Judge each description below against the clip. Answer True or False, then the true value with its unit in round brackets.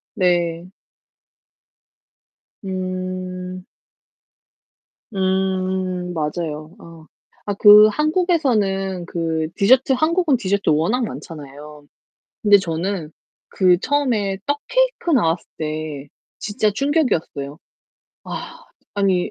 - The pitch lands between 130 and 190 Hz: True (185 Hz)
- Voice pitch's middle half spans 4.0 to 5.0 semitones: True (4.5 semitones)